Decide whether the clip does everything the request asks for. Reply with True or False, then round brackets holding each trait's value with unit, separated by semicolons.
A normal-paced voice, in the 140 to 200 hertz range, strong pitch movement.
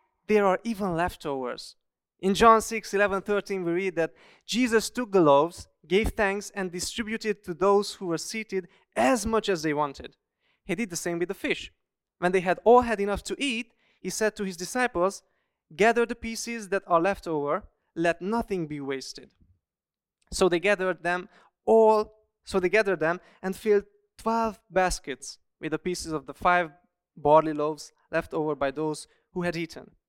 False (175 wpm; 190 Hz; 4.2 semitones)